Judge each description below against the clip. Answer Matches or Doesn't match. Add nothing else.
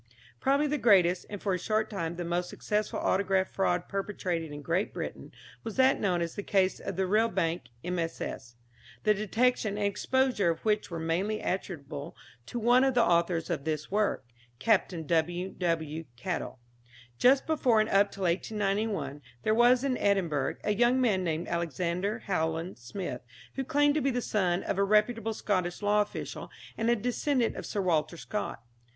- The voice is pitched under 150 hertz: Doesn't match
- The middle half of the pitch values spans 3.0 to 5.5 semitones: Matches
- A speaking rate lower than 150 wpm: Doesn't match